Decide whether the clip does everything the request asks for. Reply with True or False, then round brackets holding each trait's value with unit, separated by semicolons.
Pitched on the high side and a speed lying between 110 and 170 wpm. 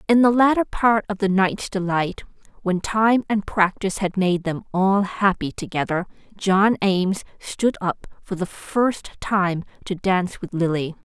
True (195 Hz; 160 wpm)